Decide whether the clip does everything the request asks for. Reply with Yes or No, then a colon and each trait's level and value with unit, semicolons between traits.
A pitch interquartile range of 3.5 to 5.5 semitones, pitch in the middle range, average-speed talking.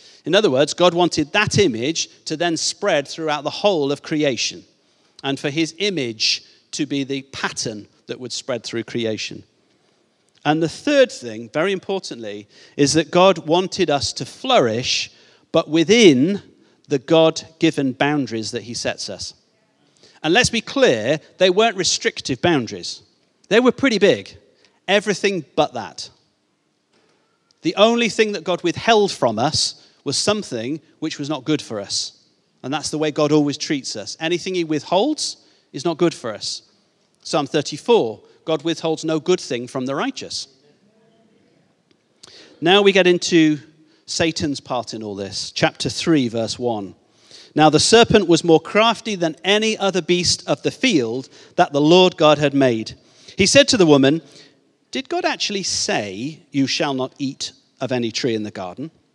Yes: average, 5.2 semitones; medium, 160 Hz; average, 160 wpm